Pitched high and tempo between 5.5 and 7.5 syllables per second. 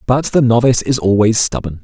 No: low, 120 Hz; 5.9 syllables/s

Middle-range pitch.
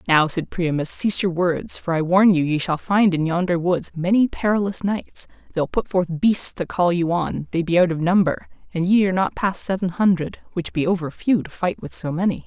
Yes: medium, 180 Hz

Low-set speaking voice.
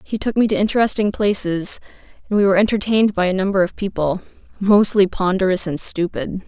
No: high, 195 Hz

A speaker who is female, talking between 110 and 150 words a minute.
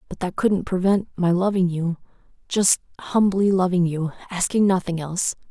Yes: female; average, 140 wpm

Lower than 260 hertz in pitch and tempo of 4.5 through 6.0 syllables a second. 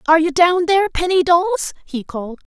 No: very high, 330 Hz; 5.6 syllables/s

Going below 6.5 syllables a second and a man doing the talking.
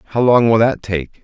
Yes: 5.3 syllables/s; male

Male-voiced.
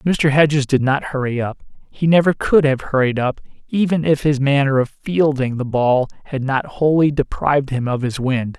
Yes: male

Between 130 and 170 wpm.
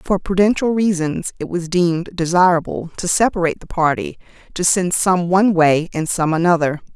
Yes: average, 165 wpm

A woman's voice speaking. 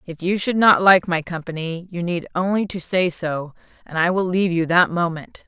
Yes: female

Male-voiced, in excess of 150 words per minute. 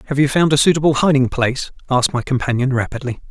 Yes: male; average, 200 wpm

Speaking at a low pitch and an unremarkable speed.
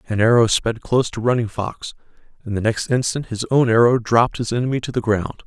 No: low, 115 Hz; fast, 220 wpm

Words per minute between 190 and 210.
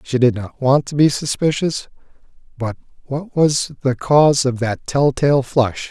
No: average, 175 wpm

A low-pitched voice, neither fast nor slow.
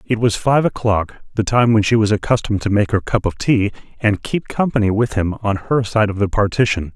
No: low, 110 Hz; fast, 235 wpm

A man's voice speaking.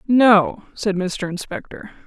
No: female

